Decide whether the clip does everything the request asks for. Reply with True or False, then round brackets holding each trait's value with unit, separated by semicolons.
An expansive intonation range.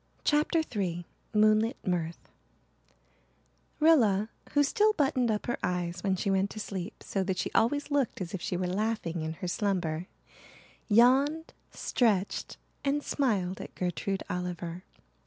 True (6.0 semitones)